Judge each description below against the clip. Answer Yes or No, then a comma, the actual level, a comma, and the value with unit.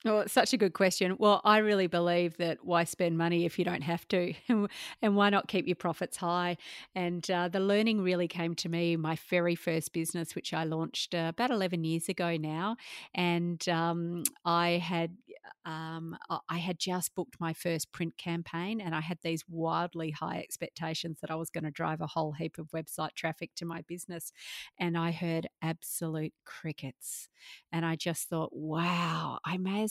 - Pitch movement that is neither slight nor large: No, narrow, 1.7 semitones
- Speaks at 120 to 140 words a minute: No, average, 190 wpm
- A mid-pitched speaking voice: Yes, medium, 170 Hz